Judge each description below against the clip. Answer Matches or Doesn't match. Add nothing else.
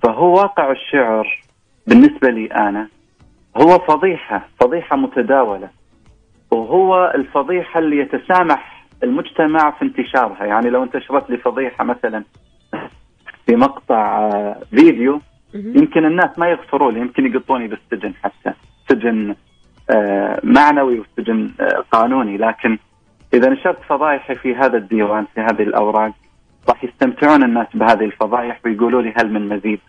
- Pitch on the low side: Matches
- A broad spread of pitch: Matches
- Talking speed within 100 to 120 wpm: Matches